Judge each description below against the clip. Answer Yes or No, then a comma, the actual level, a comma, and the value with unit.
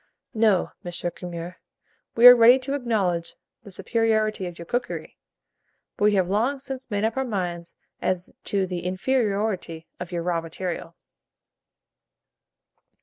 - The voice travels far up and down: No, average, 4.6 semitones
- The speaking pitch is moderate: No, high, 195 Hz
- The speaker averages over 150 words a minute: No, average, 145 wpm